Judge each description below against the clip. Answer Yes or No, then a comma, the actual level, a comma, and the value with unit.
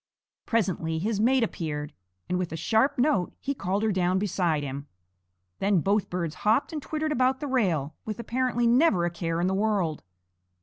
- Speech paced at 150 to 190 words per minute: Yes, average, 180 wpm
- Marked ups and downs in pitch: Yes, wide, 5.9 semitones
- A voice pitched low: No, high, 200 Hz